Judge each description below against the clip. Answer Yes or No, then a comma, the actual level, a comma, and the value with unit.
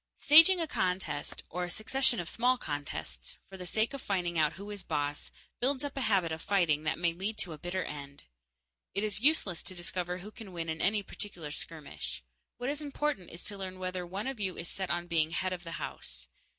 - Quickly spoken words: Yes, fast, 220 wpm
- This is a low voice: No, medium, 185 Hz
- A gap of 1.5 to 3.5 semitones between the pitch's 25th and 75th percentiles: No, average, 4.5 semitones